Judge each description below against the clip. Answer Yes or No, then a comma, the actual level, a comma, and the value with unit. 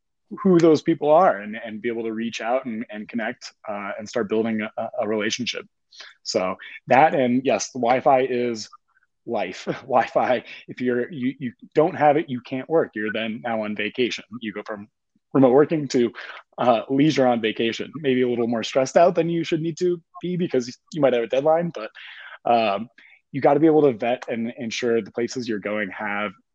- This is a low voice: Yes, low, 125 Hz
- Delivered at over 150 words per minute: Yes, average, 200 wpm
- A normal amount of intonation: Yes, average, 4.7 semitones